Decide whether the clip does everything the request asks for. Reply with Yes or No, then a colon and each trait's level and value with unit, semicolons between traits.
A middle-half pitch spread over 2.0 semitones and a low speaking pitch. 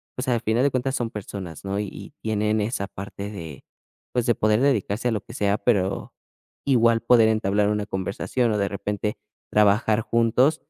Yes: average, 2.7 semitones; low, 105 Hz